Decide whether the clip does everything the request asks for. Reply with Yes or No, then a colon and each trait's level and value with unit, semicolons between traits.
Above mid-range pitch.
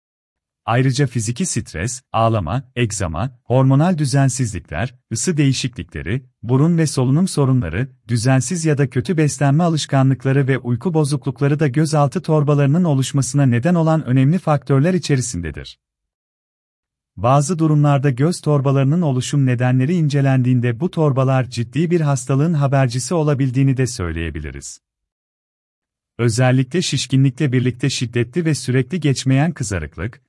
No: low, 135 Hz